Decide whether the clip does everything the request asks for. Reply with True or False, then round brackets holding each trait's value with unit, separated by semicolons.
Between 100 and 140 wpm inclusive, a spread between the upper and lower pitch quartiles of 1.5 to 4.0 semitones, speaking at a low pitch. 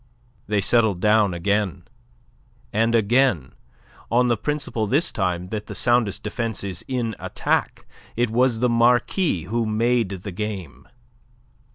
True (135 wpm; 3.5 semitones; 110 Hz)